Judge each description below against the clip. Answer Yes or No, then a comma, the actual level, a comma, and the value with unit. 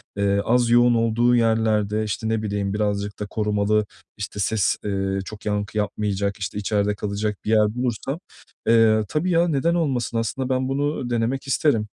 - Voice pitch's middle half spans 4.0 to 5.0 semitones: No, average, 2.9 semitones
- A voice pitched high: No, low, 110 Hz